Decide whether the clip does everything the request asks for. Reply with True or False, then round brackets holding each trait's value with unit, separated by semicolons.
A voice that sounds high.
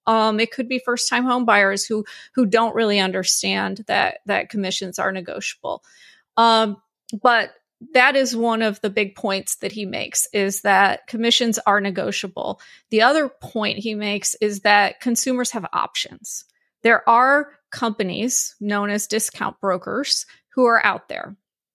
True (220 Hz)